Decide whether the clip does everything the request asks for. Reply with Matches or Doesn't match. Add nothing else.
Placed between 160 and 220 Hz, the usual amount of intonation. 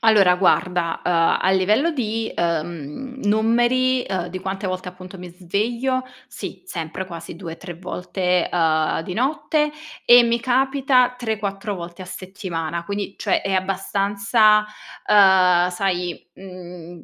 Matches